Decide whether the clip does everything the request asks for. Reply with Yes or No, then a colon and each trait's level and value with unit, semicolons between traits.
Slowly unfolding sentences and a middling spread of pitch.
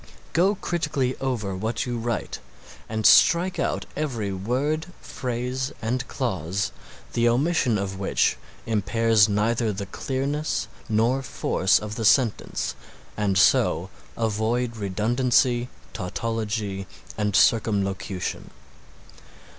Yes: slow, 105 wpm; average, 3.8 semitones